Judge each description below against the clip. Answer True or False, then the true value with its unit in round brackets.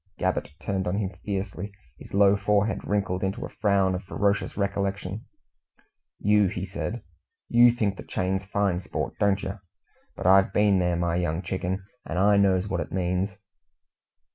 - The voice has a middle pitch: False (95 Hz)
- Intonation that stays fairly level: True (1.6 semitones)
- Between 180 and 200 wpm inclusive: False (165 wpm)